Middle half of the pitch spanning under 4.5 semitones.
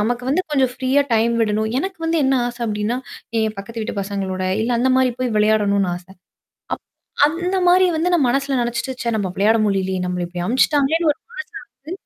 No: wide, 5.4 semitones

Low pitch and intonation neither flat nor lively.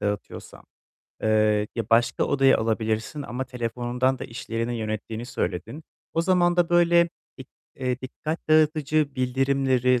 Yes: low, 125 Hz; average, 4.6 semitones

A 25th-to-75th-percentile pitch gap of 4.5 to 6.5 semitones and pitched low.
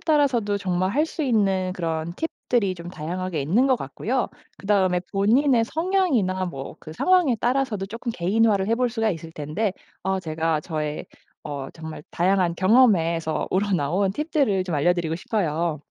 No: wide, 5.6 semitones; high, 190 Hz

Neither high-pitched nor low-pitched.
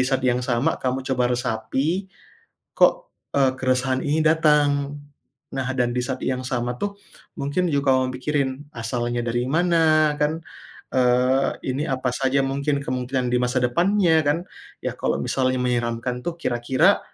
No: low, 130 Hz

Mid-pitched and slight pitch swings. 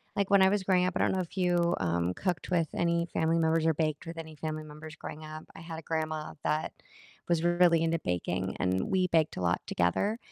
Yes: medium, 160 Hz; narrow, 2.1 semitones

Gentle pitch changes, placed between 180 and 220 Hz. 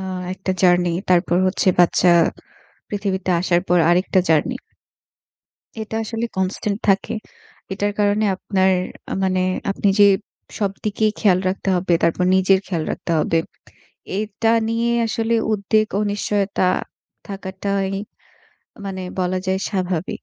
Yes: narrow, 2.0 semitones; high, 190 Hz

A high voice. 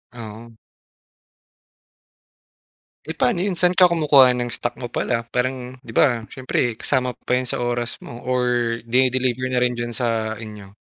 No: low, 125 Hz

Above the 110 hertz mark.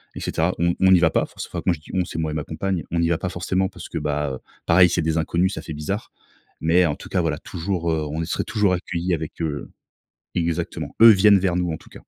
No: very low, 85 Hz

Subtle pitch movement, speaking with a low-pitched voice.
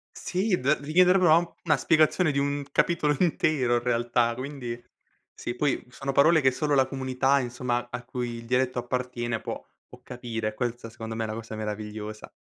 No: average, 3.5 semitones; low, 125 Hz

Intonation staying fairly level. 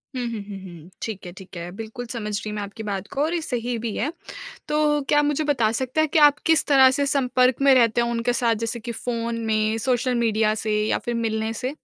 No: average, 3.2 semitones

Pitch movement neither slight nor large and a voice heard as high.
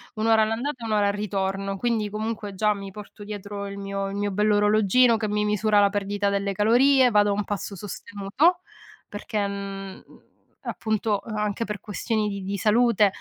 No: narrow, 1.5 semitones; high, 205 Hz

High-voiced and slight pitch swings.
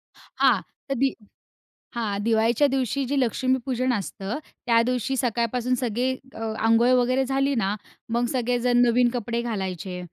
Yes: high, 240 Hz; narrow, 2.1 semitones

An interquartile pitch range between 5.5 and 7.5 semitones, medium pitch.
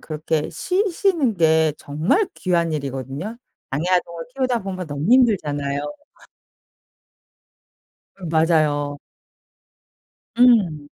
Yes: wide, 7.2 semitones; medium, 165 Hz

